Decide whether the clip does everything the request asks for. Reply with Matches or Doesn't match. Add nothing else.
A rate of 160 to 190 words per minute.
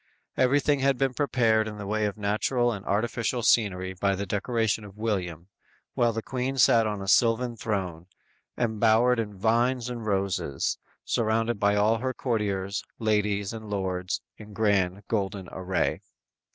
Doesn't match